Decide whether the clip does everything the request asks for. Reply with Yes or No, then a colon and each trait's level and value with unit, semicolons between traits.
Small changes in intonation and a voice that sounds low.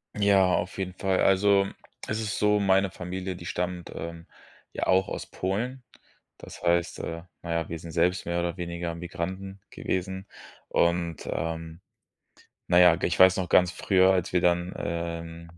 Yes: narrow, 2.0 semitones; very low, 90 Hz